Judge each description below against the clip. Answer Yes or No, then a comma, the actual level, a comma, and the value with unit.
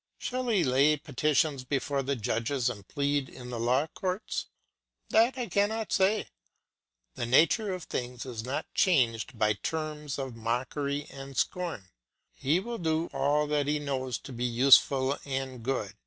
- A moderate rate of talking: Yes, average, 155 wpm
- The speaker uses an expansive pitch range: No, average, 3.9 semitones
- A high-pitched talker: No, medium, 140 Hz